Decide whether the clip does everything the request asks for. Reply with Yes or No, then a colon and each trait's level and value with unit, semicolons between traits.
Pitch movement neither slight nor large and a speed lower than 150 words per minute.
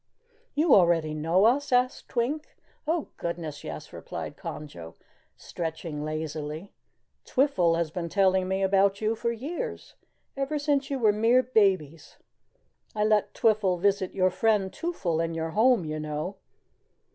No: wide, 6.3 semitones; average, 140 wpm